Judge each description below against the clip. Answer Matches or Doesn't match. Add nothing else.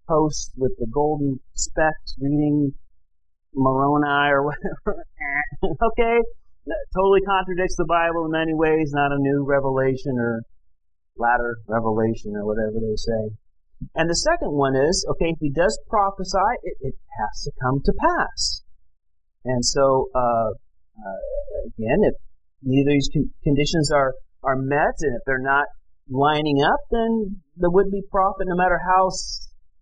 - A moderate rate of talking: Matches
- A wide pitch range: Matches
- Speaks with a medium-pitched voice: Matches